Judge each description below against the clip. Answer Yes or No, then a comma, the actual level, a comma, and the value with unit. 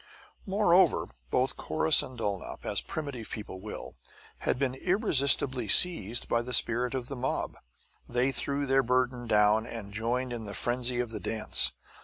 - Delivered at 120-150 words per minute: No, average, 160 wpm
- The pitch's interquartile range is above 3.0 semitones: No, average, 2.7 semitones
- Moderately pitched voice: No, low, 125 Hz